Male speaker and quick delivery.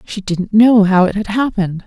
No: female; fast, 225 wpm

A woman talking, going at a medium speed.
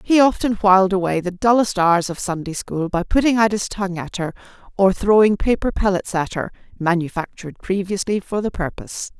Yes: female; average, 185 wpm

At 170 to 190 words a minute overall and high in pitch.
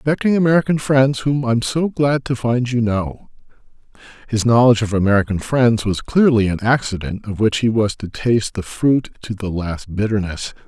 No: average, 180 wpm; low, 115 Hz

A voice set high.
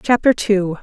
Yes: high, 205 Hz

